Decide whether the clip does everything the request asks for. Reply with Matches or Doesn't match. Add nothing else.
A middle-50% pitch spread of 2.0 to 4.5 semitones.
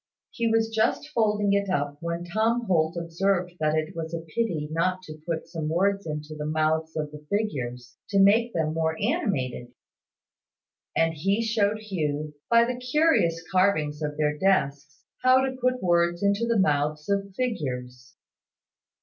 Doesn't match